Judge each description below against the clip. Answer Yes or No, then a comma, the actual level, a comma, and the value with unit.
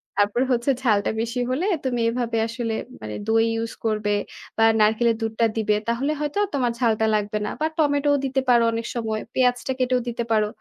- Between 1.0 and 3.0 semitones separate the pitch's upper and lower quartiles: Yes, narrow, 2.4 semitones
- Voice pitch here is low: No, high, 230 Hz